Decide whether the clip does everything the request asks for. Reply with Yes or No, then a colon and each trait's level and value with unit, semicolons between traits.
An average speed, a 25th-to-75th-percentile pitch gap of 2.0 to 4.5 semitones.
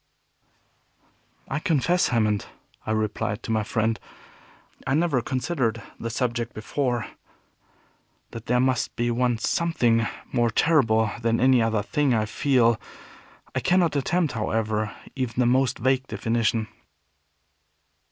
No: slow, 125 wpm; average, 2.9 semitones